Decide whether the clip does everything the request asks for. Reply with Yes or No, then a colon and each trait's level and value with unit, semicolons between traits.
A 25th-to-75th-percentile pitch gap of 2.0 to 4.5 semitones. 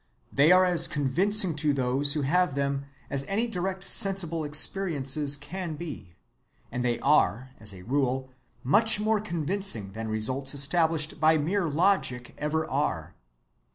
No: average, 5.2 semitones